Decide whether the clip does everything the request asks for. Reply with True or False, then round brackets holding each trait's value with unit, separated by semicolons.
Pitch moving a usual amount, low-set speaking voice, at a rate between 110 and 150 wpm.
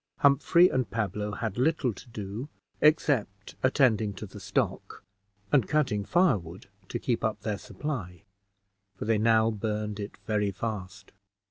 True (4.1 semitones; 110 Hz; 140 wpm)